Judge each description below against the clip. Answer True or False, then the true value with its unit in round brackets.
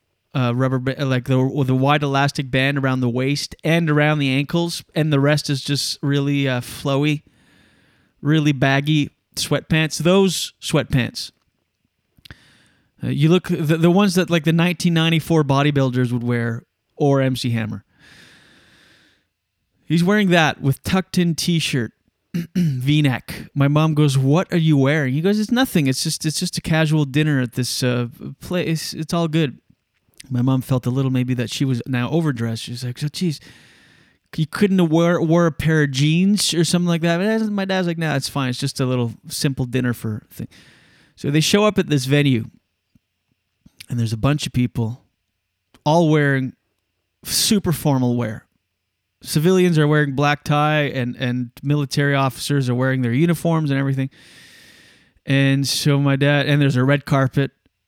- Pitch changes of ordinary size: True (4.0 semitones)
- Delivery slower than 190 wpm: True (165 wpm)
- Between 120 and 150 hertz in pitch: True (140 Hz)